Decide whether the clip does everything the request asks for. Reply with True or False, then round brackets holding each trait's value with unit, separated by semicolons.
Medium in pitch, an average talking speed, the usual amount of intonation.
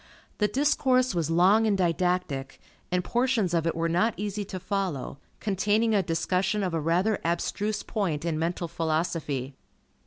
True (180 Hz; 155 wpm; 4.0 semitones)